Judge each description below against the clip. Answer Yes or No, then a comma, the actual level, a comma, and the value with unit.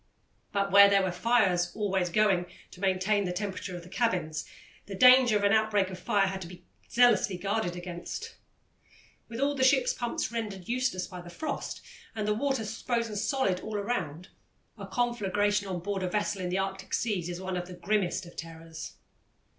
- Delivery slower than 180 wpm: No, average, 185 wpm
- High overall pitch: Yes, high, 195 Hz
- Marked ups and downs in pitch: No, average, 3.4 semitones